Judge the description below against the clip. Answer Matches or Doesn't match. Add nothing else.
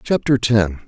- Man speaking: Matches